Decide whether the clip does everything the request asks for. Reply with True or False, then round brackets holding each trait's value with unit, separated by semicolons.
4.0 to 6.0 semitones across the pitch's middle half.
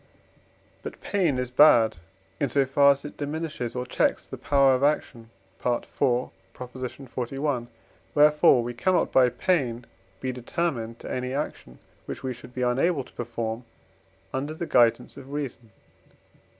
False (3.0 semitones)